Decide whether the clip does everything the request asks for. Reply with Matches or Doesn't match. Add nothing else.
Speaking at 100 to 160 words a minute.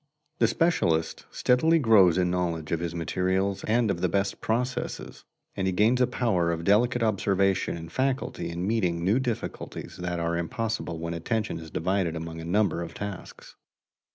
Doesn't match